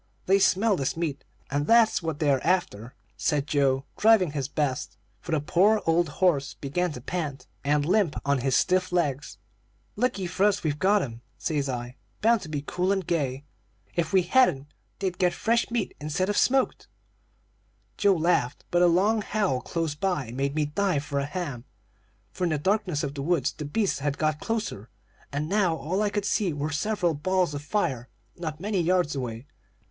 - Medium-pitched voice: Yes, medium, 165 Hz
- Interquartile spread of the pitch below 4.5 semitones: No, average, 5.0 semitones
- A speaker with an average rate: Yes, average, 190 wpm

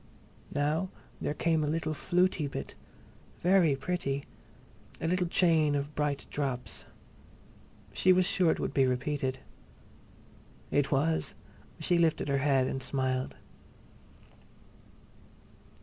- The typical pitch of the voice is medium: Yes, medium, 150 Hz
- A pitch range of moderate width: Yes, average, 3.6 semitones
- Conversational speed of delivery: No, slow, 105 wpm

